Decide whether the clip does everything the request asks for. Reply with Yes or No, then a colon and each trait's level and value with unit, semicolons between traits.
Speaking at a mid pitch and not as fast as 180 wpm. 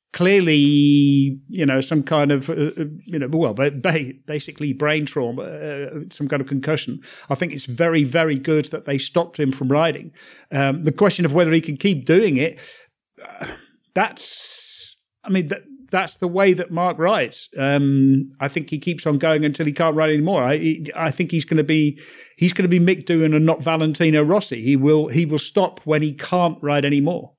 No: medium, 155 Hz; average, 195 wpm